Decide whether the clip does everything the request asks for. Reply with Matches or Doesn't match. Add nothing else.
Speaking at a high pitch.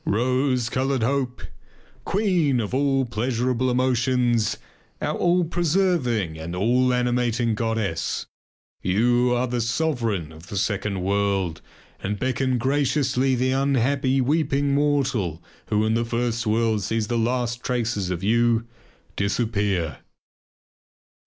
Doesn't match